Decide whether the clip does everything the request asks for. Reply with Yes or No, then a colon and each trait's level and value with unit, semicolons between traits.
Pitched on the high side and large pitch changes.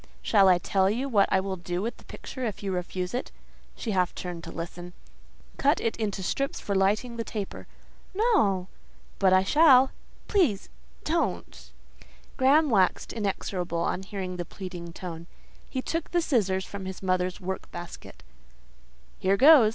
No: high, 195 Hz; average, 4.5 semitones